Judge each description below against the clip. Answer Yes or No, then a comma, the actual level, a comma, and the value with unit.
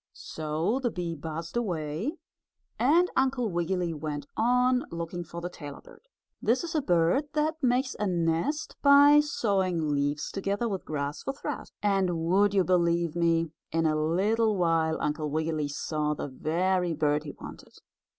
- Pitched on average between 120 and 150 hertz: No, medium, 175 Hz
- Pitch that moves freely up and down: Yes, wide, 6.5 semitones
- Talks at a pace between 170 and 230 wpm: No, average, 160 wpm